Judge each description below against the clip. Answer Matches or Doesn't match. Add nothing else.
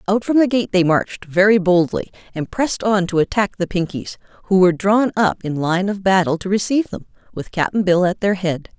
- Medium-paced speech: Doesn't match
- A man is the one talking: Doesn't match